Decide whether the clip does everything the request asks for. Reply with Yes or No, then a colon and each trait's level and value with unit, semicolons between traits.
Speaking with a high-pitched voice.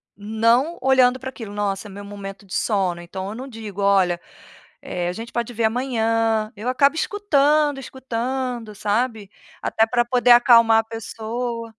Yes: high, 225 Hz